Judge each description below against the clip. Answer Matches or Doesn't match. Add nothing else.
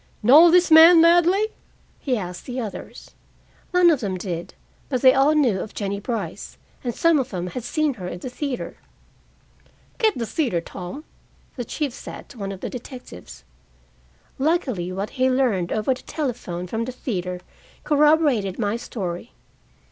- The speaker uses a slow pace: Doesn't match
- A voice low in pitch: Doesn't match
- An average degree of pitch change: Doesn't match